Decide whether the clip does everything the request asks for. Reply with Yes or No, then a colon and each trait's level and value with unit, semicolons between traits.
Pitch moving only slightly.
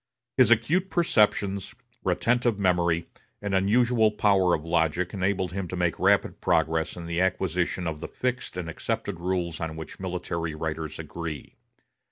No: average, 3.6 semitones